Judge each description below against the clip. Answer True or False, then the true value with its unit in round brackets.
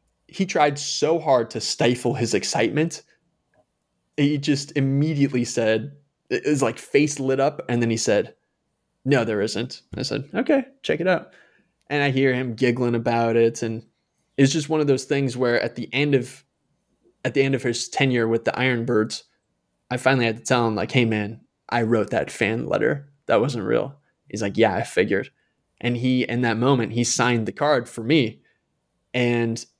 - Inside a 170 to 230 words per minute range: True (185 wpm)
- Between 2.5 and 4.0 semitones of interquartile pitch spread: True (3.3 semitones)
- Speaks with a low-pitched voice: True (125 Hz)